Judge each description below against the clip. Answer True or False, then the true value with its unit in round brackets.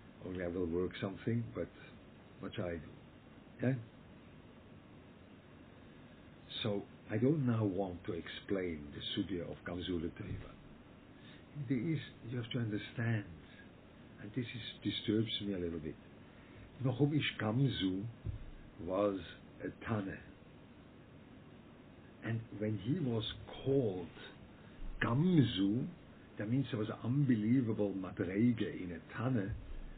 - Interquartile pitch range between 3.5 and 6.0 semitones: True (4.3 semitones)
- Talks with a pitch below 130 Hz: True (105 Hz)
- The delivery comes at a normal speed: False (110 wpm)